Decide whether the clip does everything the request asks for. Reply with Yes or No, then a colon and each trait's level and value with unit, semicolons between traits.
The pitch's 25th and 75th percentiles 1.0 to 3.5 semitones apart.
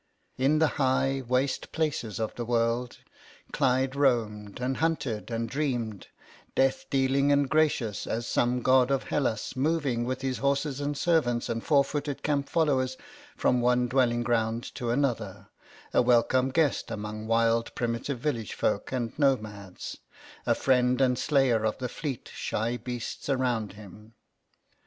Yes: average, 3.0 semitones